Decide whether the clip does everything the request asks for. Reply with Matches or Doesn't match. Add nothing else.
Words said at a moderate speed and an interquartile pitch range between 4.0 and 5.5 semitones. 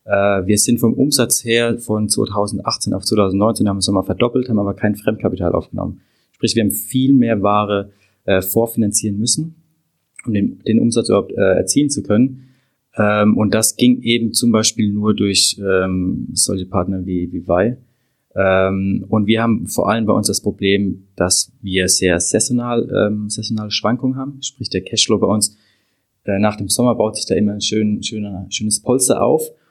Doesn't match